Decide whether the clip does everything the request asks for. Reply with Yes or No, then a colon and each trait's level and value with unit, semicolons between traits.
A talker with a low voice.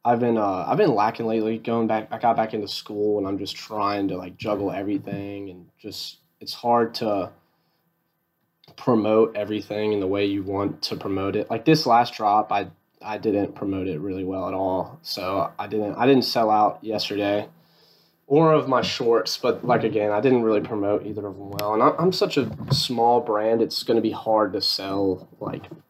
Yes: low, 105 Hz